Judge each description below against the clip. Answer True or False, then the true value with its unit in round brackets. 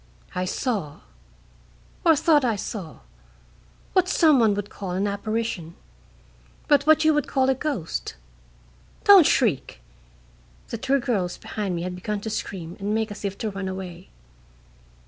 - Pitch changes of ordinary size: False (6.1 semitones)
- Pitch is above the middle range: True (210 Hz)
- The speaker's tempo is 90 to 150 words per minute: True (145 wpm)